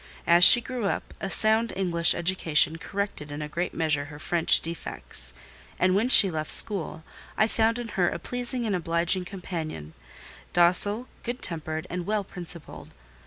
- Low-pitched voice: No, medium, 175 Hz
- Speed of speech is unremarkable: Yes, average, 165 wpm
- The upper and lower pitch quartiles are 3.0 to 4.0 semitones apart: No, average, 4.6 semitones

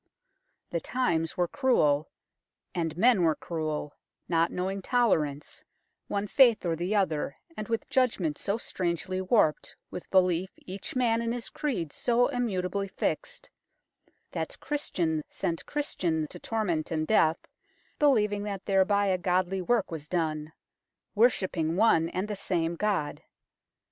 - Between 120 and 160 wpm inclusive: Yes, average, 140 wpm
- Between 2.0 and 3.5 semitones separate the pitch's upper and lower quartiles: No, average, 5.2 semitones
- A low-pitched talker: No, medium, 185 Hz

